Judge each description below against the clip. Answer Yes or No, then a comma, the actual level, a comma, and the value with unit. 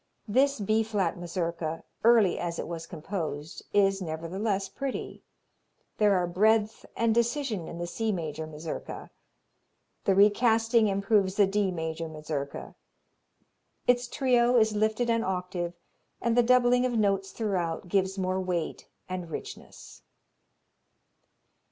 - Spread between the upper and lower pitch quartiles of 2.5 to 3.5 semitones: No, average, 4.6 semitones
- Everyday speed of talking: No, slow, 125 wpm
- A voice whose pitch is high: Yes, high, 195 Hz